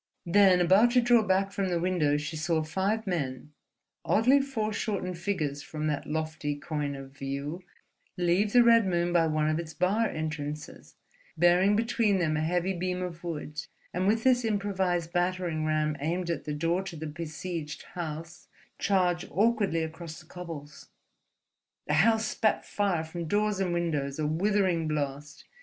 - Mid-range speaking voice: Yes, medium, 175 Hz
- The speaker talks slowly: No, average, 160 wpm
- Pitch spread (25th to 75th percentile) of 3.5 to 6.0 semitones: Yes, average, 4.0 semitones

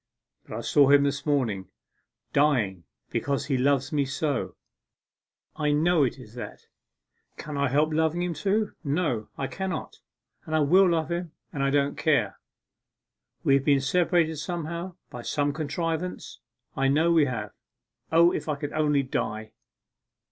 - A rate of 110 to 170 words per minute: Yes, average, 155 wpm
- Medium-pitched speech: Yes, medium, 145 Hz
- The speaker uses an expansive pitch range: No, average, 3.1 semitones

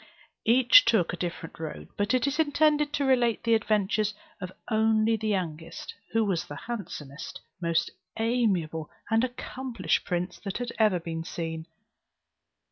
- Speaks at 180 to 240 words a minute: No, average, 145 wpm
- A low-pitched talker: No, high, 215 Hz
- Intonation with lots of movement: Yes, wide, 5.9 semitones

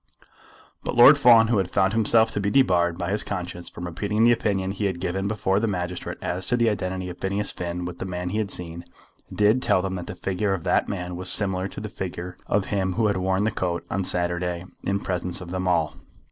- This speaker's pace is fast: Yes, fast, 235 wpm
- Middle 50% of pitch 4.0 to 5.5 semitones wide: No, narrow, 2.6 semitones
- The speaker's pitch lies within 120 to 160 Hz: No, very low, 95 Hz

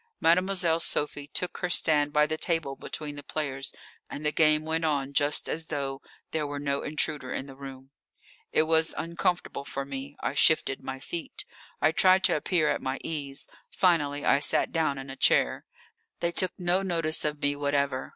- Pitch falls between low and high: Yes, medium, 150 Hz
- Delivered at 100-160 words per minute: No, average, 185 wpm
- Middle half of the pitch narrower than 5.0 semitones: Yes, narrow, 2.6 semitones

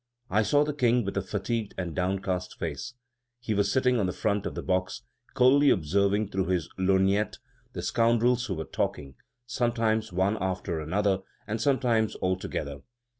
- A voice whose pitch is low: Yes, low, 100 Hz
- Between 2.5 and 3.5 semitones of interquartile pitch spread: No, average, 4.0 semitones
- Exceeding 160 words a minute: Yes, average, 170 wpm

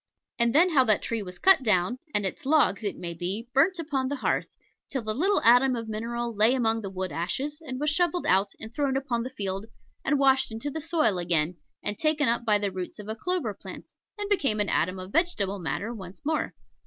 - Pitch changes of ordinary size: No, wide, 6.1 semitones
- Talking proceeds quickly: Yes, fast, 225 wpm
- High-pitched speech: Yes, high, 230 Hz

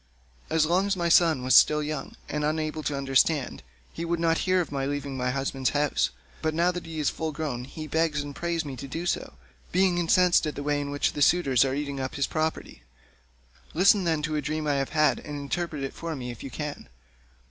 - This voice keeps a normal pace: No, fast, 235 wpm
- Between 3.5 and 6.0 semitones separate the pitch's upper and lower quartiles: No, average, 2.9 semitones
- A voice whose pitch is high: No, medium, 150 Hz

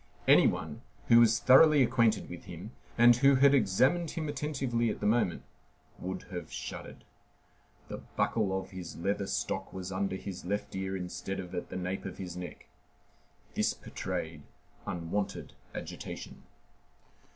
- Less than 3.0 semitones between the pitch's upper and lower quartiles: No, average, 4.8 semitones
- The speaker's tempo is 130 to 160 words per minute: Yes, average, 150 wpm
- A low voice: Yes, low, 100 Hz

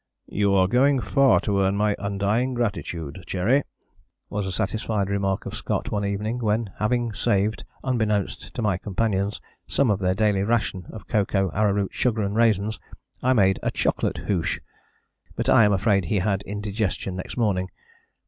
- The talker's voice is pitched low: Yes, low, 105 Hz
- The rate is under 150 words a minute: No, average, 165 wpm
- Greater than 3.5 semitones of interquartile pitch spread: No, narrow, 2.4 semitones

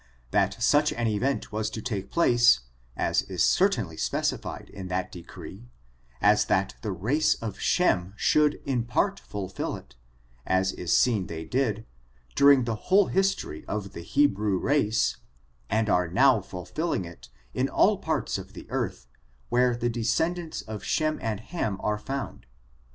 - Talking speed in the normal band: Yes, average, 155 wpm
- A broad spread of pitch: Yes, wide, 6.3 semitones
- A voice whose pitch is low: Yes, low, 110 Hz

